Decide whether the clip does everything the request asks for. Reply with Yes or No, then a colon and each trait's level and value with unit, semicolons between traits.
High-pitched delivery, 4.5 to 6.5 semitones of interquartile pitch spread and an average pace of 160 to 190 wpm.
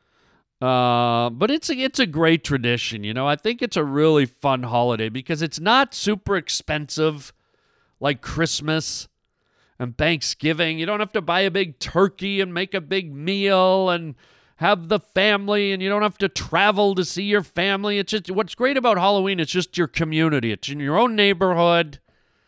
No: medium, 170 Hz; average, 5.3 semitones; average, 175 wpm